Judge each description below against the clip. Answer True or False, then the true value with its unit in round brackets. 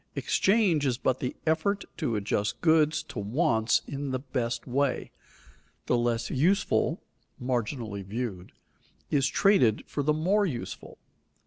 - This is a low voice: True (130 Hz)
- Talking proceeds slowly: True (130 wpm)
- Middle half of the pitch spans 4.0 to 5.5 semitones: True (5.2 semitones)